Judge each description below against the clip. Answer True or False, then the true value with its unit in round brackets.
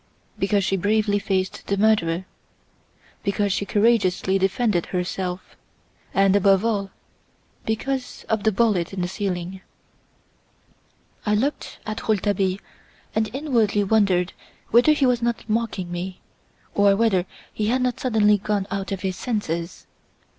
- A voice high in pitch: True (205 Hz)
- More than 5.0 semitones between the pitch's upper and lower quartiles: False (2.6 semitones)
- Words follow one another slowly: True (130 wpm)